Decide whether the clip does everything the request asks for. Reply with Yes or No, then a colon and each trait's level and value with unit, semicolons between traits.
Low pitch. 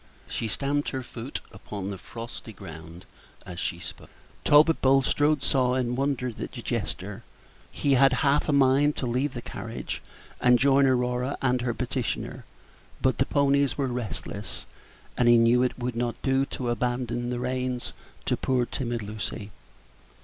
Yes: low, 125 Hz